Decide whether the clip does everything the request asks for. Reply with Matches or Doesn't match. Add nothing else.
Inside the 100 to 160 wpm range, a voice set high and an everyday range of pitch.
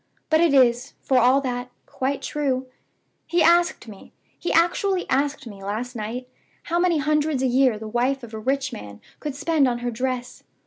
Doesn't match